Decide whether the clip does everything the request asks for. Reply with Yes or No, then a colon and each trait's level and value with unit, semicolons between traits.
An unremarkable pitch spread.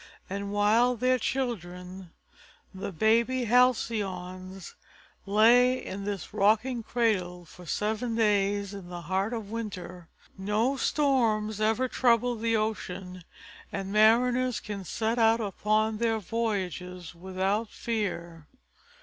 Yes: average, 3.6 semitones